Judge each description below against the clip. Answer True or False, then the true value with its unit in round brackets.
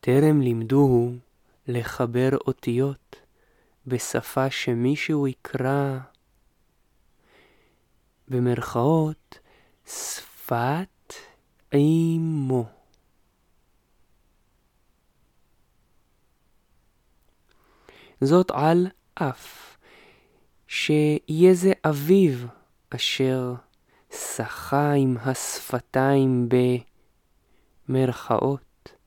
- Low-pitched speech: True (130 Hz)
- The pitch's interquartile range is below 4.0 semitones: True (3.6 semitones)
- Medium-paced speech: False (45 wpm)